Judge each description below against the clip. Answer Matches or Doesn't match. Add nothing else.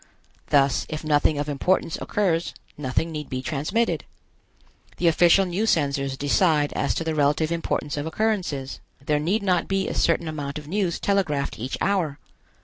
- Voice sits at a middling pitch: Matches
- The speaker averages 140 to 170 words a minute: Matches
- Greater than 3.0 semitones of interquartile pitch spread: Matches